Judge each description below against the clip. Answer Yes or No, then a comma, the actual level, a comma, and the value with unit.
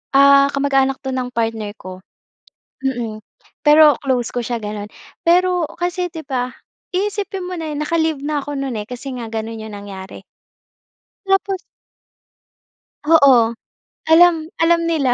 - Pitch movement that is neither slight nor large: No, wide, 6.0 semitones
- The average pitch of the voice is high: Yes, very high, 275 Hz